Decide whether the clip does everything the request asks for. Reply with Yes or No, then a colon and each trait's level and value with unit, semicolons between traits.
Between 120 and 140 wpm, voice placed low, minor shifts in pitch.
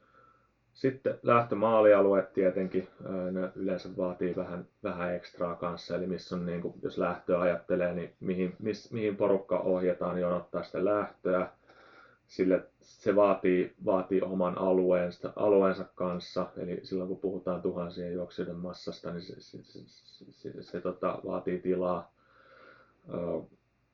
Yes: average, 135 wpm; very low, 90 Hz; narrow, 1.6 semitones